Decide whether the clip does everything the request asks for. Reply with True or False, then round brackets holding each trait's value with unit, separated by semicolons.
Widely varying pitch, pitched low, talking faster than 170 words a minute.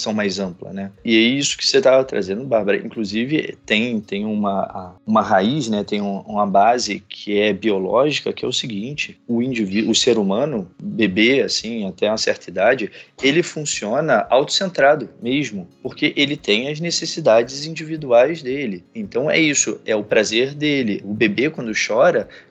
False (6.7 semitones; 125 Hz; 165 wpm)